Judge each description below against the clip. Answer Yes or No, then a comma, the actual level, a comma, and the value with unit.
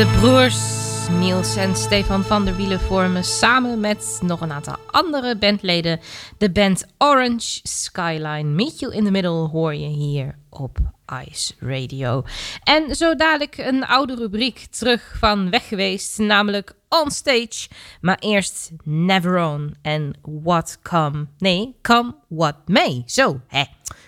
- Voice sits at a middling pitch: Yes, medium, 175 Hz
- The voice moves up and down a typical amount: No, wide, 7.2 semitones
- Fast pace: No, slow, 135 wpm